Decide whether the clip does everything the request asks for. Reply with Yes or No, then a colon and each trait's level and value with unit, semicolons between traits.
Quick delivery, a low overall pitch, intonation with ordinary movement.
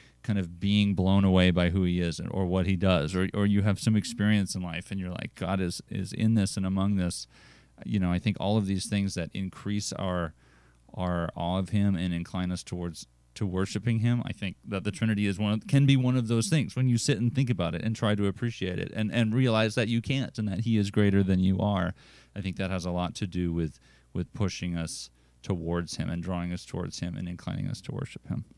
Yes: fast, 250 wpm; very low, 95 Hz; average, 3.1 semitones